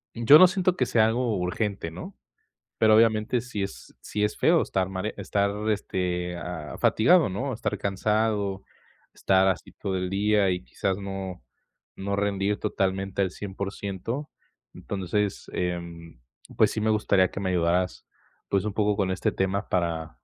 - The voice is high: No, low, 100 Hz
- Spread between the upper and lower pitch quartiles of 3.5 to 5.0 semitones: No, narrow, 2.5 semitones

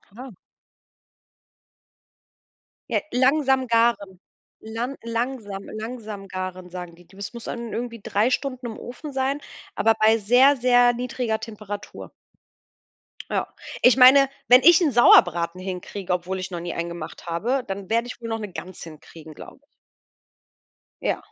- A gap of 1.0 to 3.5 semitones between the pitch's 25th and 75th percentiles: No, average, 5.0 semitones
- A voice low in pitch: No, high, 225 Hz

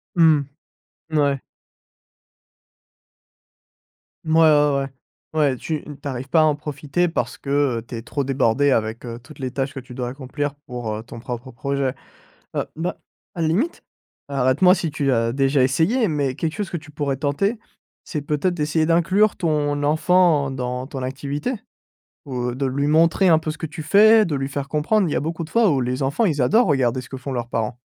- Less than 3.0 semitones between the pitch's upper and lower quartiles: No, average, 3.5 semitones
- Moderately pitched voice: Yes, medium, 145 Hz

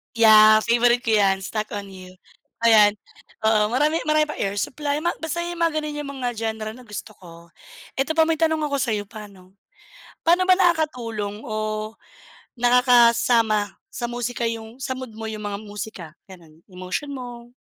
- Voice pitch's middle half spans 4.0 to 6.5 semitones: Yes, average, 4.6 semitones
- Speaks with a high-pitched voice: Yes, high, 230 Hz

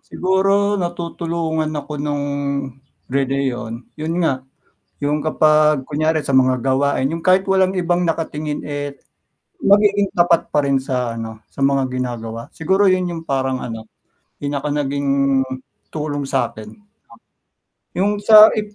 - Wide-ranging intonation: No, average, 4.7 semitones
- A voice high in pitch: No, medium, 150 Hz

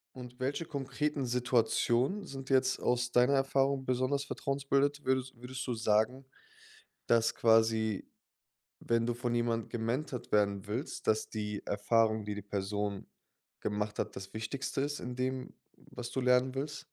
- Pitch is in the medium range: No, low, 125 Hz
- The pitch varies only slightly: No, average, 3.3 semitones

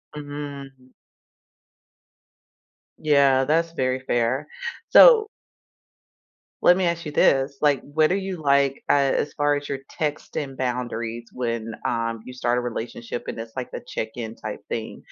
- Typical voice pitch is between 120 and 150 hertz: Yes, low, 135 Hz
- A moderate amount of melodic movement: Yes, average, 3.4 semitones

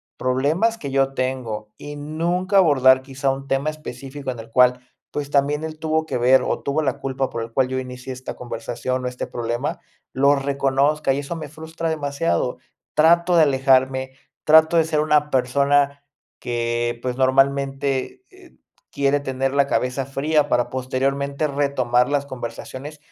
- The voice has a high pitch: No, low, 135 Hz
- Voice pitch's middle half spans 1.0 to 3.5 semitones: Yes, narrow, 2.5 semitones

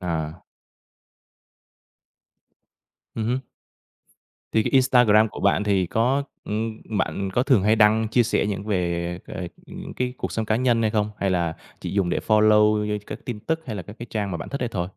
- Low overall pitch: Yes, low, 105 Hz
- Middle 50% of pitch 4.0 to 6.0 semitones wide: No, average, 2.8 semitones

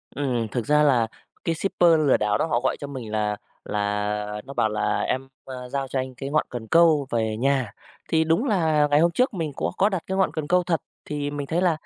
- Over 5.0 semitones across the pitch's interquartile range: Yes, wide, 5.5 semitones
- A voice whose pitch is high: No, medium, 140 Hz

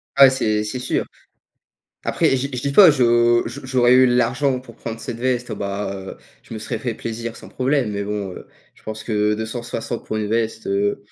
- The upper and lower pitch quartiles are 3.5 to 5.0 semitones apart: No, average, 2.9 semitones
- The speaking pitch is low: Yes, low, 115 Hz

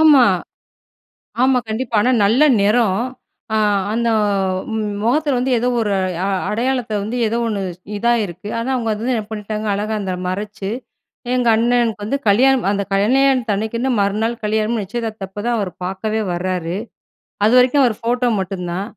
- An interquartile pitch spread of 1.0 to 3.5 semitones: Yes, average, 3.1 semitones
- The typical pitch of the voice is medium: No, high, 220 Hz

